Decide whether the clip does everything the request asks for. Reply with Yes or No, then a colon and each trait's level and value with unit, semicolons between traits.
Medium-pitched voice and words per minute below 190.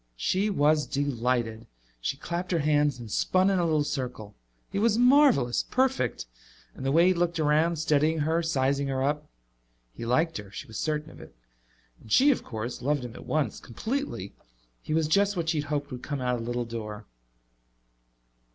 No: medium, 150 Hz; average, 195 wpm